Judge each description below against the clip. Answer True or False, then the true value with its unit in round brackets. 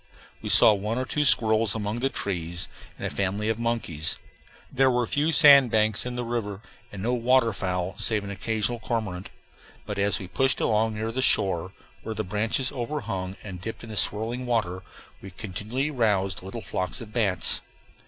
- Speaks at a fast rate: False (185 wpm)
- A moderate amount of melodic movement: True (3.7 semitones)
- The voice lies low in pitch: True (110 Hz)